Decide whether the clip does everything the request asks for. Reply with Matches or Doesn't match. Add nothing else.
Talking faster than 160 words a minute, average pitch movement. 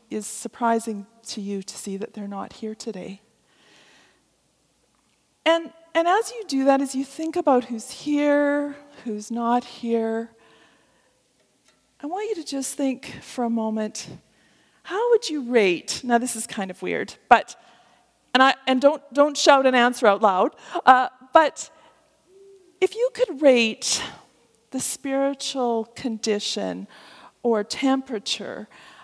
Doesn't match